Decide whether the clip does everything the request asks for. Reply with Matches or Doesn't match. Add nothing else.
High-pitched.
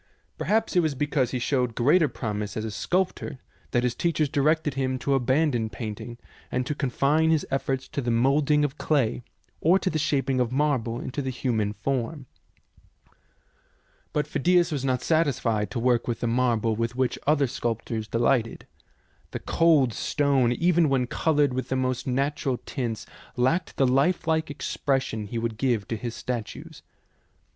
Doesn't match